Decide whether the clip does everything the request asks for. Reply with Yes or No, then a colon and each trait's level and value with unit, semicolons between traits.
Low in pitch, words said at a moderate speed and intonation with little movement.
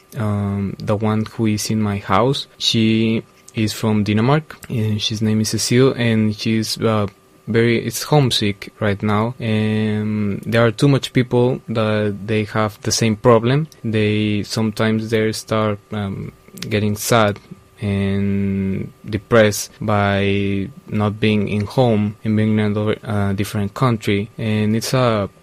Yes: low, 110 Hz; average, 140 wpm; narrow, 1.5 semitones